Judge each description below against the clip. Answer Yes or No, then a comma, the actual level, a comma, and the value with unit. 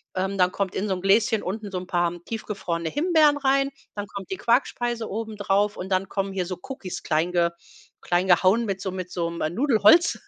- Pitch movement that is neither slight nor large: Yes, average, 3.7 semitones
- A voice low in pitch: No, high, 195 Hz